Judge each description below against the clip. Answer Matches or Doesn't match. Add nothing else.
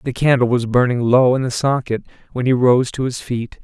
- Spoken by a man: Matches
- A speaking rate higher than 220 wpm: Matches